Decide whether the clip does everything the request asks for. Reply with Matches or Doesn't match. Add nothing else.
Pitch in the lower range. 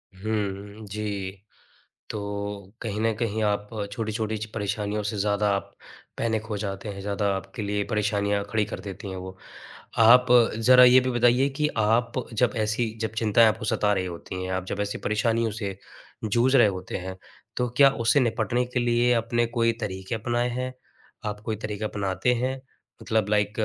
Matches